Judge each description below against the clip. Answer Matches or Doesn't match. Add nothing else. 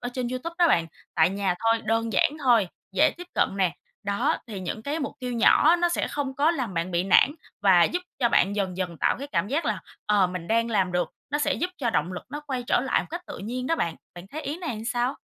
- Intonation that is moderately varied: Doesn't match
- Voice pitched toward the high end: Matches